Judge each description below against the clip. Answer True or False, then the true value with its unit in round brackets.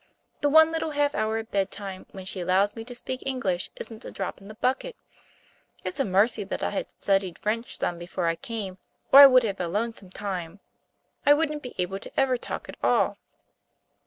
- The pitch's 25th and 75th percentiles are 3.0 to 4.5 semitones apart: False (5.2 semitones)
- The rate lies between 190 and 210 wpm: True (205 wpm)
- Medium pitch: False (210 Hz)